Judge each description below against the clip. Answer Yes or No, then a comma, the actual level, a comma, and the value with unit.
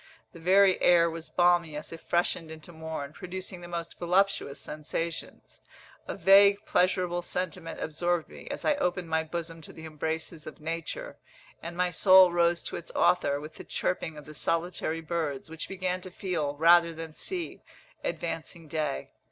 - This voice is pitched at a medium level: Yes, medium, 170 Hz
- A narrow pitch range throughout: Yes, narrow, 2.1 semitones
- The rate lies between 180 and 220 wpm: No, average, 170 wpm